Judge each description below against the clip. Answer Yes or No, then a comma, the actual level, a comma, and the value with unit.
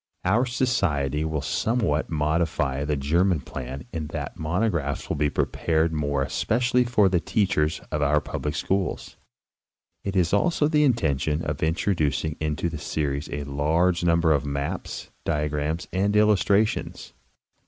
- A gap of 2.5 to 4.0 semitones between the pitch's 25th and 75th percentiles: No, average, 4.8 semitones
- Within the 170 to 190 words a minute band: No, average, 150 wpm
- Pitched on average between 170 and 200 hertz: No, very low, 80 Hz